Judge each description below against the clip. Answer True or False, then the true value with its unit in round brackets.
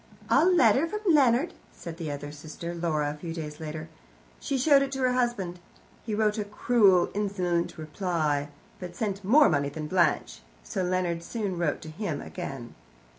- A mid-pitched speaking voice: True (180 Hz)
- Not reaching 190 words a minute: True (175 wpm)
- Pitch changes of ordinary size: False (6.6 semitones)